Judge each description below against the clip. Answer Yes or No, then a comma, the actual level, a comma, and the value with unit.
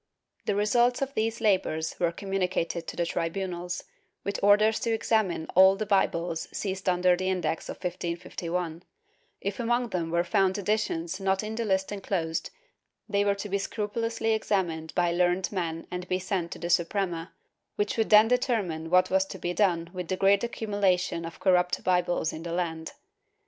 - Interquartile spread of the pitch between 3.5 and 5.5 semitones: No, average, 3.1 semitones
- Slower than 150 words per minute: No, average, 175 wpm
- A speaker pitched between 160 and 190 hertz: Yes, medium, 185 Hz